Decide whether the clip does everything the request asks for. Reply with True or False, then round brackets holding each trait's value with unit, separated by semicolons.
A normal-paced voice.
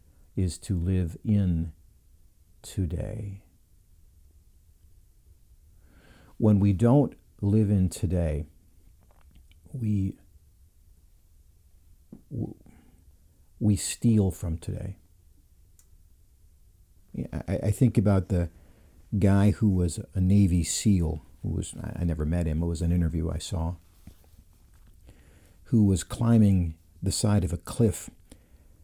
False (95 wpm)